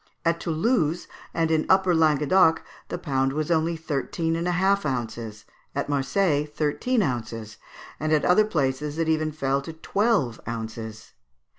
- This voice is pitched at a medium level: Yes, medium, 155 Hz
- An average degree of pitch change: Yes, average, 4.0 semitones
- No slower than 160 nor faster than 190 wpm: No, average, 150 wpm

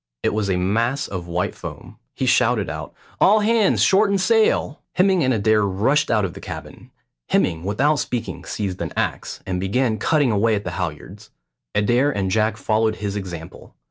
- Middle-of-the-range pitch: No, low, 110 Hz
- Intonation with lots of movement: Yes, wide, 6.9 semitones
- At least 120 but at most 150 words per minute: No, average, 175 wpm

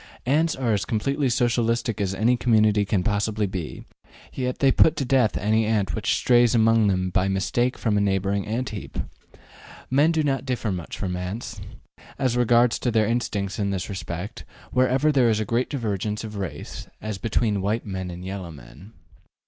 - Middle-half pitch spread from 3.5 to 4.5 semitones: Yes, average, 3.8 semitones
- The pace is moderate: Yes, average, 180 wpm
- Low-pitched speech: Yes, low, 110 Hz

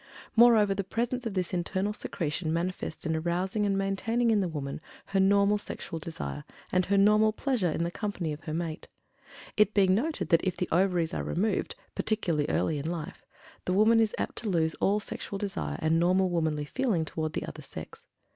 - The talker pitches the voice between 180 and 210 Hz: Yes, medium, 185 Hz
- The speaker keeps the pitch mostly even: No, average, 4.1 semitones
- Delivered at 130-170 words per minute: No, average, 195 wpm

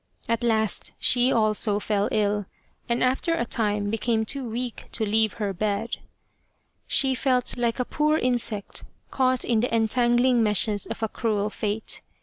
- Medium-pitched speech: No, high, 225 Hz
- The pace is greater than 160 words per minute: No, average, 155 wpm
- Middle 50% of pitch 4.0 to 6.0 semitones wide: No, average, 2.7 semitones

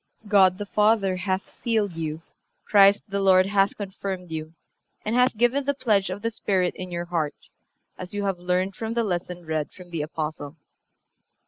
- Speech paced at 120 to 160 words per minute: No, average, 180 wpm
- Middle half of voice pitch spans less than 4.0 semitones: Yes, average, 2.9 semitones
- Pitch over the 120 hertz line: Yes, high, 190 Hz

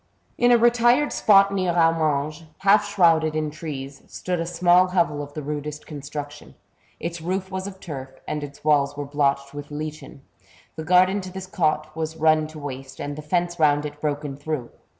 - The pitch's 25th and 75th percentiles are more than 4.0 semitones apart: No, average, 3.6 semitones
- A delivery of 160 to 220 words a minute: Yes, average, 185 wpm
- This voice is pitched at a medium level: Yes, medium, 155 Hz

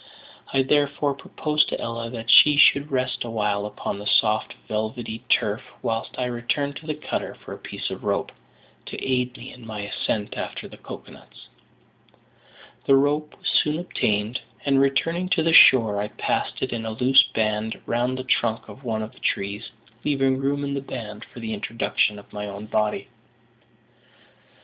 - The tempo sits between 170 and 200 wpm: Yes, average, 180 wpm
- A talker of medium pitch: No, low, 120 Hz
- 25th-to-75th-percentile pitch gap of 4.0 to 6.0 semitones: Yes, average, 4.3 semitones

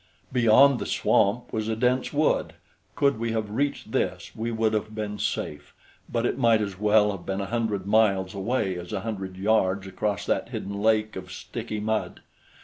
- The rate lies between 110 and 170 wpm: No, average, 185 wpm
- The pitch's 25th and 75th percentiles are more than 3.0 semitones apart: No, narrow, 2.5 semitones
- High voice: No, low, 110 Hz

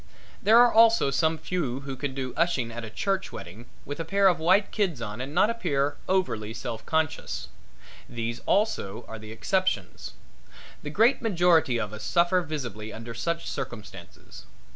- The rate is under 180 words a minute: Yes, average, 165 wpm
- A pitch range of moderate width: No, wide, 7.9 semitones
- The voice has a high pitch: No, medium, 145 Hz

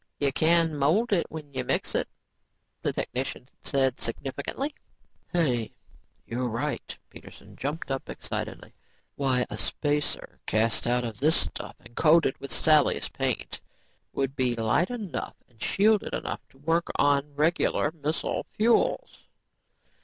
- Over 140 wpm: No, slow, 135 wpm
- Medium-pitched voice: Yes, medium, 145 Hz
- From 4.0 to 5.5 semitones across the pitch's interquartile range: Yes, average, 4.5 semitones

